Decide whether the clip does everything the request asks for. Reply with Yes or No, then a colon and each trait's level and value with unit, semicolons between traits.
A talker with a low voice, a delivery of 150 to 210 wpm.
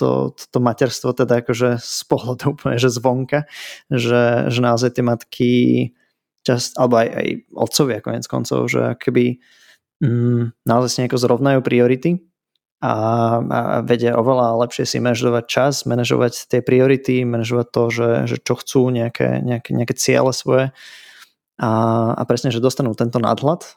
No: low, 120 Hz; average, 140 wpm